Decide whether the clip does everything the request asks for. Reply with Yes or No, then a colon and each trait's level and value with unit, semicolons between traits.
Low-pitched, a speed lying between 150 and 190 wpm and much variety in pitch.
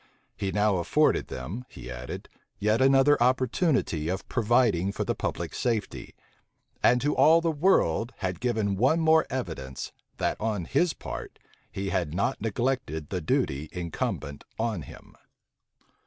No: low, 105 Hz; average, 140 wpm; wide, 6.9 semitones